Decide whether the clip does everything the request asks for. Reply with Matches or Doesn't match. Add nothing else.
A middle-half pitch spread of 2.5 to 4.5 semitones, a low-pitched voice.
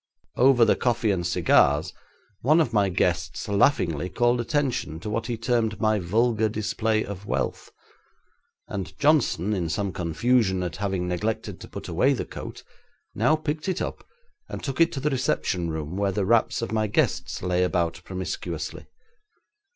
Doesn't match